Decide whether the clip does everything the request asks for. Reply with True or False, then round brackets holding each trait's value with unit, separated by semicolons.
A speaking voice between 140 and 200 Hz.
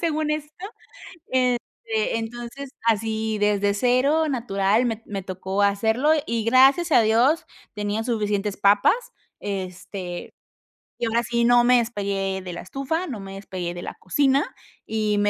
False (225 Hz)